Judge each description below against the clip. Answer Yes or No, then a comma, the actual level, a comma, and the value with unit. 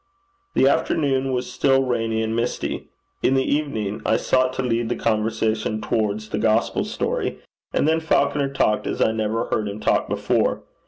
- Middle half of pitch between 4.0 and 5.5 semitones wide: No, average, 3.6 semitones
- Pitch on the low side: Yes, low, 115 Hz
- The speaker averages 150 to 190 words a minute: Yes, average, 170 wpm